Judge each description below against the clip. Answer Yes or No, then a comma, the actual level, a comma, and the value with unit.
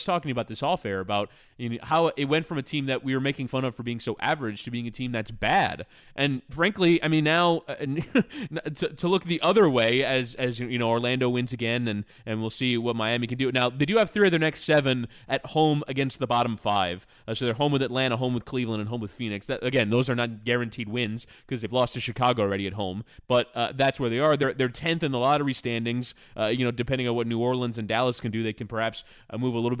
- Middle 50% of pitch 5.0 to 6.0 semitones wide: No, average, 3.2 semitones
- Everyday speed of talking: No, fast, 265 wpm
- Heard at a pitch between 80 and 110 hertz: No, low, 125 Hz